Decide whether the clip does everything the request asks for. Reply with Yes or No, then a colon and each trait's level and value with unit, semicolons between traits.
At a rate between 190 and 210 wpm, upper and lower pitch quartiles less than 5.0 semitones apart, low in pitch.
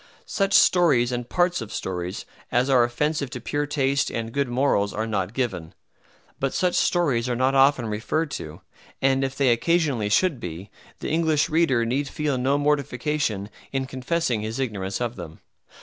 No: average, 170 wpm; average, 4.2 semitones; low, 130 Hz